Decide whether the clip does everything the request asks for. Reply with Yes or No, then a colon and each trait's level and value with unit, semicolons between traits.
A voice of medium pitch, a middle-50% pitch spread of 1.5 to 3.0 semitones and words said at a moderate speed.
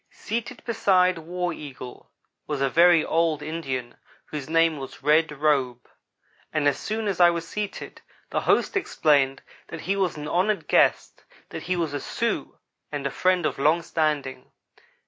No: medium, 160 Hz; average, 3.8 semitones; average, 165 wpm